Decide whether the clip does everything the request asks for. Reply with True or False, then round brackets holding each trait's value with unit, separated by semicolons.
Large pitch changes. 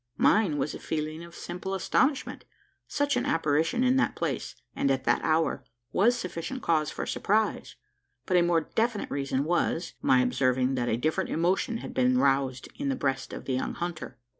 True (6.8 semitones)